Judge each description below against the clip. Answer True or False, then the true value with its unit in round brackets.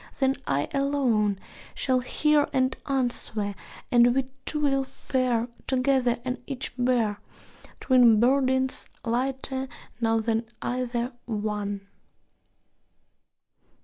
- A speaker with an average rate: False (100 wpm)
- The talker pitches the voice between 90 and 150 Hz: False (250 Hz)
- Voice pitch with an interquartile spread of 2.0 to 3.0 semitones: True (2.7 semitones)